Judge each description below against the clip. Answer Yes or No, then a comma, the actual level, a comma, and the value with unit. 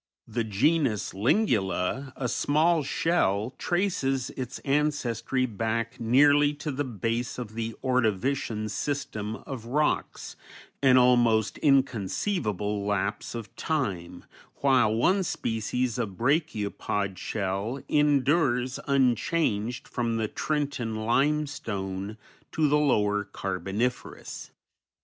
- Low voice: Yes, low, 120 Hz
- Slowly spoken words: Yes, slow, 100 wpm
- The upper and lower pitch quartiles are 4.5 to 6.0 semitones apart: Yes, average, 4.9 semitones